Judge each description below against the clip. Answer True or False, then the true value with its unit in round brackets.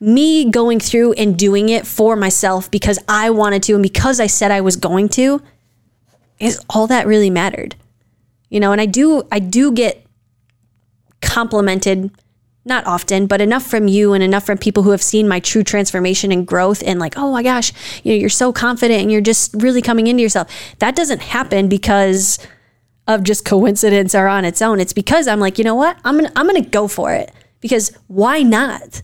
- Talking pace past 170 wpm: True (200 wpm)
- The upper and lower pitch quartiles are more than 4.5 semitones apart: False (3.3 semitones)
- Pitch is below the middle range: False (205 Hz)